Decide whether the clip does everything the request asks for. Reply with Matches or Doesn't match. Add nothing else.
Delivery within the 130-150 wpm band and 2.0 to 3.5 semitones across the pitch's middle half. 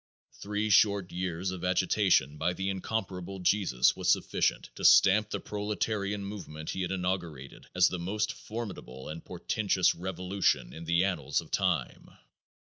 Matches